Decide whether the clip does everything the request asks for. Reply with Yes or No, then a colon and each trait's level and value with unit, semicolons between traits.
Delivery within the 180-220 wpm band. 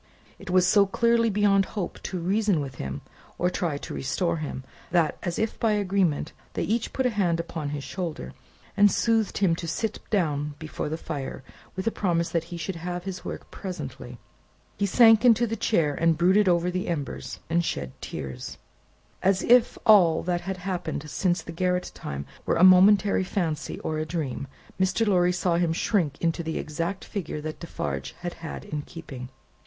Yes: average, 185 wpm